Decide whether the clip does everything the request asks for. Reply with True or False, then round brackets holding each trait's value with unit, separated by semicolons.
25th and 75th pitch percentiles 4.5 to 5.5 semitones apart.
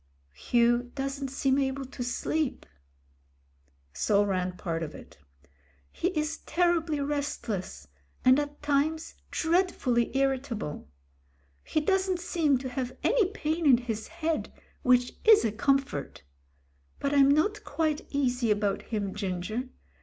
True (4.8 semitones)